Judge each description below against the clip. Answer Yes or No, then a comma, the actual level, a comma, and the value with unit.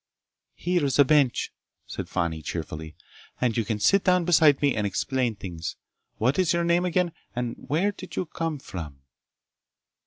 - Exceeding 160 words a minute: No, average, 155 wpm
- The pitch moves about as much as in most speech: No, wide, 8.9 semitones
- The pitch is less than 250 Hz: Yes, low, 135 Hz